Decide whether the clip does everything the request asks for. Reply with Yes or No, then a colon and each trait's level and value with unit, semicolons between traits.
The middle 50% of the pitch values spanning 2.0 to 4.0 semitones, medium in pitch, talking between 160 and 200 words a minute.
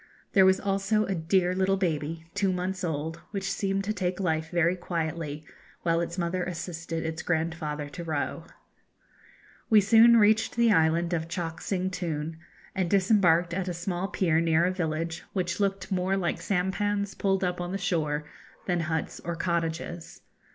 Yes: average, 2.8 semitones; medium, 175 Hz; average, 165 wpm